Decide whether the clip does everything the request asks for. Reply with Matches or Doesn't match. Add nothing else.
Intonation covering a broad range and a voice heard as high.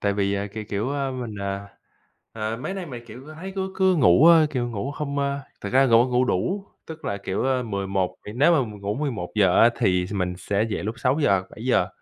Doesn't match